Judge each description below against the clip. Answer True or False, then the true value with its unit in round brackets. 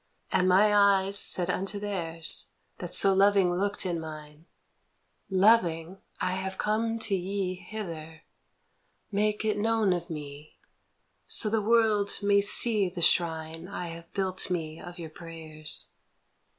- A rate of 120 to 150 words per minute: True (145 wpm)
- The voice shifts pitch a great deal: False (3.5 semitones)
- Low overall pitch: False (185 Hz)